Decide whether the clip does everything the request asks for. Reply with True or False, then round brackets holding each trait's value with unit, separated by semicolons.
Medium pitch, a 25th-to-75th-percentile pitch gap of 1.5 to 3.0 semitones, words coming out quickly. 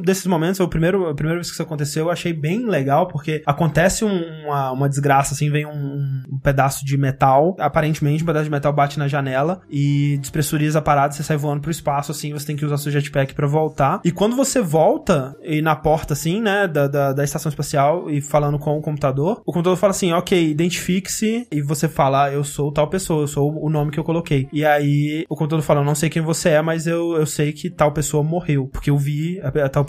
True (150 Hz; 2.5 semitones; 235 wpm)